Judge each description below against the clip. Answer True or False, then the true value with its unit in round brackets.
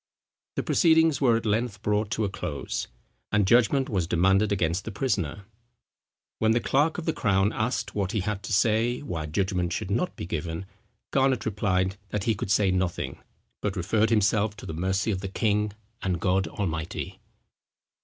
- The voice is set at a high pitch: False (105 Hz)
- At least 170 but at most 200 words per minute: True (175 wpm)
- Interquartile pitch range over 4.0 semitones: False (3.1 semitones)